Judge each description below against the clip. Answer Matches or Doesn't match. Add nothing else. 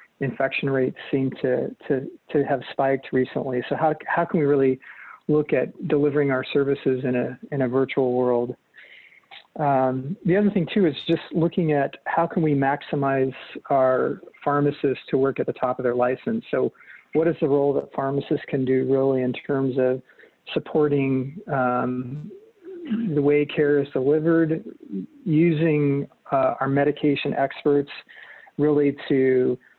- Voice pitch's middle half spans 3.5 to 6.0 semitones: Doesn't match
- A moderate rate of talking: Matches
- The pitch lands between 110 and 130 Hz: Doesn't match